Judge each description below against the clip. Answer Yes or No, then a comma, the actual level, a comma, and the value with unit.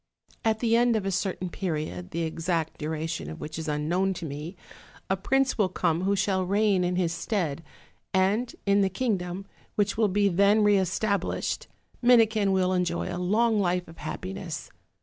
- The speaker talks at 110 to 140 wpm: No, average, 175 wpm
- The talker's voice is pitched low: No, medium, 185 Hz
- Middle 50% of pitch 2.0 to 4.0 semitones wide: Yes, average, 3.5 semitones